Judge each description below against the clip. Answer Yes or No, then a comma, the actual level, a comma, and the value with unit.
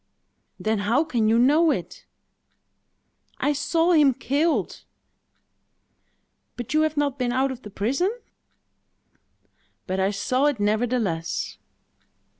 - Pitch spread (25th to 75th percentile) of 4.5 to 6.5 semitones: Yes, wide, 5.4 semitones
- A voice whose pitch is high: Yes, very high, 255 Hz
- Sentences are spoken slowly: Yes, slow, 115 wpm